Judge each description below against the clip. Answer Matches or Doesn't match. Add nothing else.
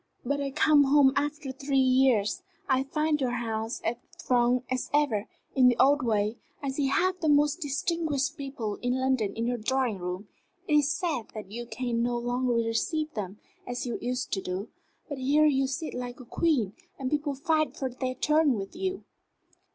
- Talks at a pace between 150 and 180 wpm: Doesn't match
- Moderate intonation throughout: Matches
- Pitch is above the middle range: Matches